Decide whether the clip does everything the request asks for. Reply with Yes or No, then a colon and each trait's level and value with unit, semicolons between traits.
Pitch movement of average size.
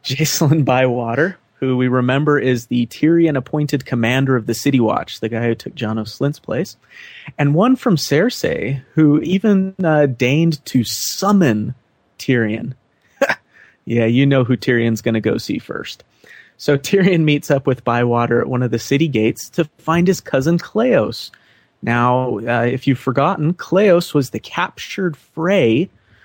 Yes: average, 4.7 semitones